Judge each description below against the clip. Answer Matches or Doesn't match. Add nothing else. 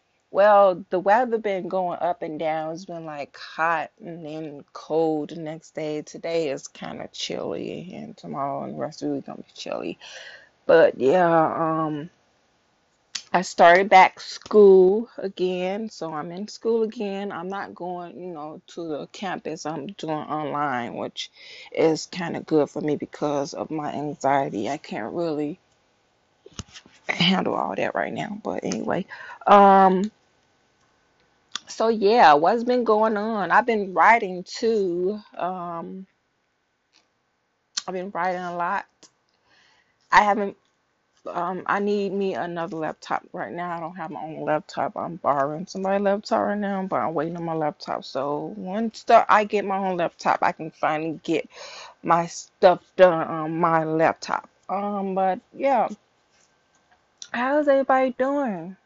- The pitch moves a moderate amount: Matches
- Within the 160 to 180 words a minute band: Doesn't match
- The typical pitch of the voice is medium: Matches